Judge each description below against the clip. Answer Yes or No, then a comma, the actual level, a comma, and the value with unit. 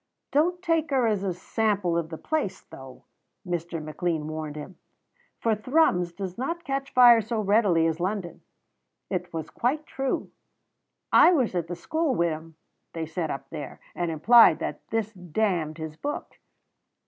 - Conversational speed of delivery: Yes, average, 160 wpm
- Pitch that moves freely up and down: Yes, wide, 6.7 semitones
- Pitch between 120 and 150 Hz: No, medium, 185 Hz